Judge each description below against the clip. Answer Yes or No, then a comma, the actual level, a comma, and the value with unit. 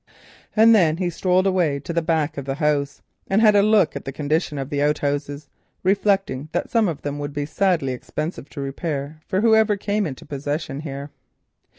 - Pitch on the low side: No, medium, 155 Hz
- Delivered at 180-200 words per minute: Yes, average, 195 wpm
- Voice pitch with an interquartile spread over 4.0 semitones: Yes, average, 4.9 semitones